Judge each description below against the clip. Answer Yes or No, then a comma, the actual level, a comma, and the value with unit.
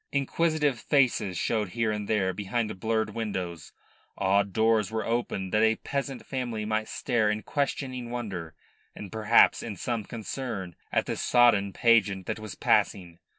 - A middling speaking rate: Yes, average, 150 wpm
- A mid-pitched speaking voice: No, low, 110 Hz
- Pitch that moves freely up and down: No, average, 3.3 semitones